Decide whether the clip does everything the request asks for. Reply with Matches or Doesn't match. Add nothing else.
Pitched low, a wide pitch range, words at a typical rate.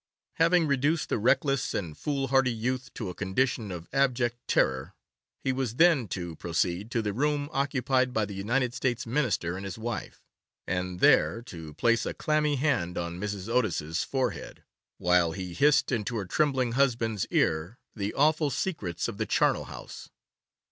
Matches